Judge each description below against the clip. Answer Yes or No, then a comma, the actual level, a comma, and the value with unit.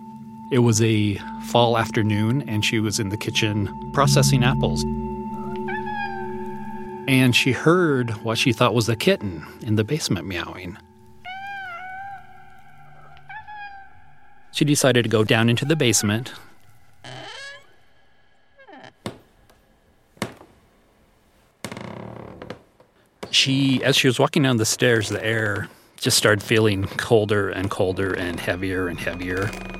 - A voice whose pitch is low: Yes, low, 110 Hz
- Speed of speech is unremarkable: No, slow, 110 wpm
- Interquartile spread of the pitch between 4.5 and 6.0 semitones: Yes, wide, 5.5 semitones